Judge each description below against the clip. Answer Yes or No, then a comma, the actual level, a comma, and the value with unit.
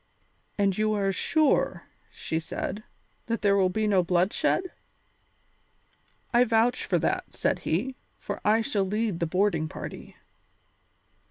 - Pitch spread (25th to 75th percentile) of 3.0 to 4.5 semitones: Yes, average, 3.4 semitones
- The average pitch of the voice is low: No, high, 205 Hz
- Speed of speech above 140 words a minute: No, slow, 135 wpm